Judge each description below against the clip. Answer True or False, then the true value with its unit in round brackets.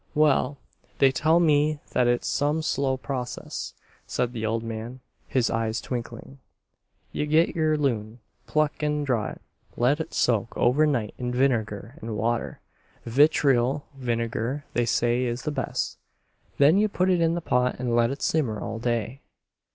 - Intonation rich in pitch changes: False (4.1 semitones)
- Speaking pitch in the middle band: False (130 Hz)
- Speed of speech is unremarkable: True (160 wpm)